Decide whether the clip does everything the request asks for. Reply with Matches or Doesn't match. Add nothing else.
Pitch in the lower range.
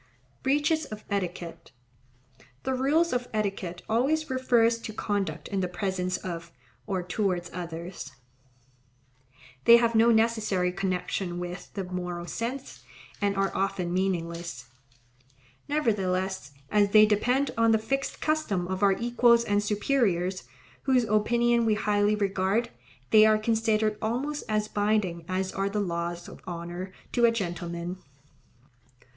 Doesn't match